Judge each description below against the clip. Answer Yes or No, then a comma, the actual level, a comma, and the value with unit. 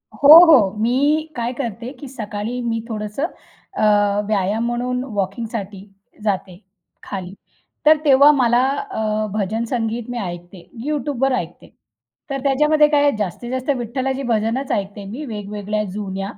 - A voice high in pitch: Yes, high, 230 Hz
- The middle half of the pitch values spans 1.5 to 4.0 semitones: No, average, 4.4 semitones